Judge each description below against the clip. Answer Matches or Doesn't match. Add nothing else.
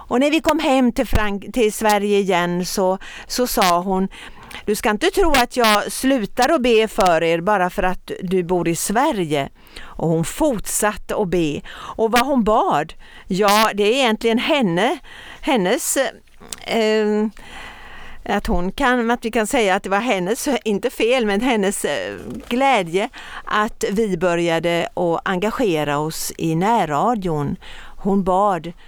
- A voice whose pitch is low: Doesn't match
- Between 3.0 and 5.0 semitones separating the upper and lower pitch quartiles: Matches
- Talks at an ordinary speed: Matches